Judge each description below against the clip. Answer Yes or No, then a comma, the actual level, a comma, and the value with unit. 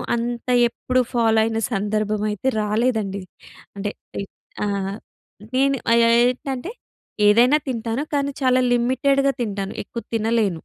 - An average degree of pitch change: Yes, average, 3.2 semitones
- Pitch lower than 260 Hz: Yes, high, 235 Hz